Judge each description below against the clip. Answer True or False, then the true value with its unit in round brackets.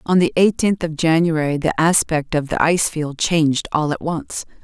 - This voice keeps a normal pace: True (195 wpm)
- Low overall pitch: False (160 Hz)